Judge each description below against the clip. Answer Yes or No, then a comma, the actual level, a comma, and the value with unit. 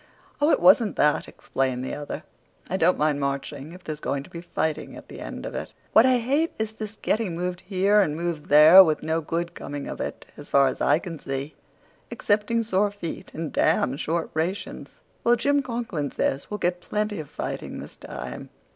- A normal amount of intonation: No, wide, 5.9 semitones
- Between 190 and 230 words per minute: Yes, average, 200 wpm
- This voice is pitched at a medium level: Yes, medium, 170 Hz